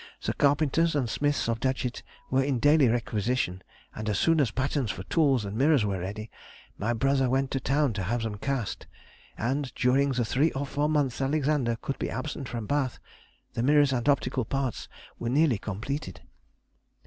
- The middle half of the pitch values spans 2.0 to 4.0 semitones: Yes, average, 3.7 semitones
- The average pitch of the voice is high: No, low, 130 Hz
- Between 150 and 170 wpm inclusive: No, average, 180 wpm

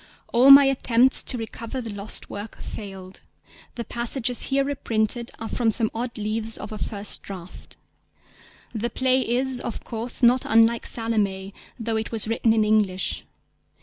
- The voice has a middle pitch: No, high, 225 Hz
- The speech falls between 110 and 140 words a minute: No, average, 155 wpm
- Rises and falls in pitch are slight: Yes, narrow, 2.3 semitones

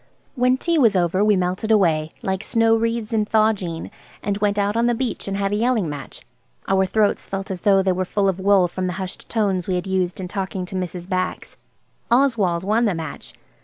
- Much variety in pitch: No, average, 3.1 semitones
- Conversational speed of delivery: No, fast, 215 wpm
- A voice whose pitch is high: Yes, high, 195 Hz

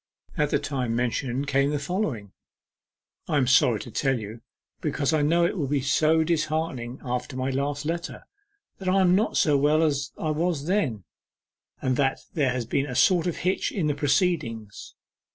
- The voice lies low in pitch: No, medium, 145 Hz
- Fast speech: No, average, 185 wpm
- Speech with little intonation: No, average, 3.9 semitones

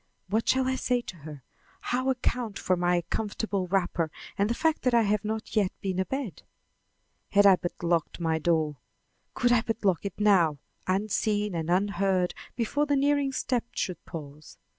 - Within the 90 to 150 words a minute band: No, average, 175 wpm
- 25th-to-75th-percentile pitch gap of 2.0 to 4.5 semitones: No, average, 5.1 semitones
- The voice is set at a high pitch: Yes, high, 200 Hz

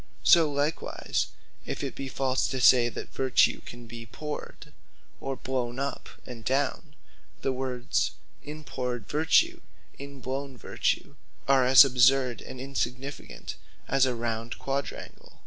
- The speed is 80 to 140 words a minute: Yes, slow, 135 wpm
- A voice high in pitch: No, low, 130 Hz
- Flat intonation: Yes, narrow, 2.0 semitones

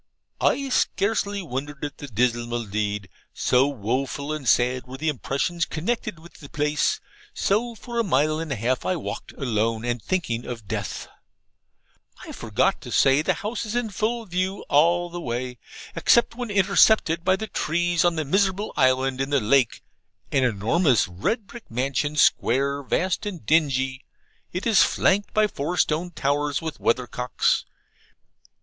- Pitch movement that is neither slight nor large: No, wide, 6.7 semitones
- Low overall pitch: No, medium, 150 Hz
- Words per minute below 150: No, average, 160 wpm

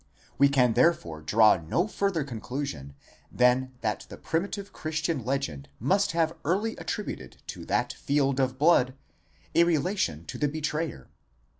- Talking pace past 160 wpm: No, average, 140 wpm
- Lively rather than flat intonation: Yes, wide, 6.7 semitones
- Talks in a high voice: No, medium, 140 Hz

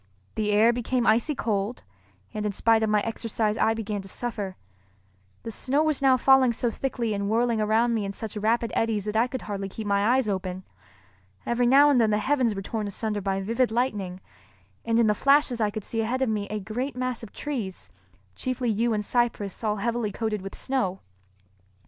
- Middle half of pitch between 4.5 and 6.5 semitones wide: No, average, 2.7 semitones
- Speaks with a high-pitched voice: Yes, high, 225 Hz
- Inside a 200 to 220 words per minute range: Yes, fast, 205 wpm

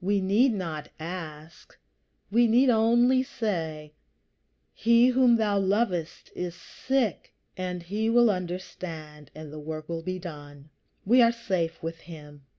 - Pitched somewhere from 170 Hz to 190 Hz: Yes, medium, 185 Hz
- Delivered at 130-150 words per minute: Yes, average, 140 wpm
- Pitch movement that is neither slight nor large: No, wide, 6.3 semitones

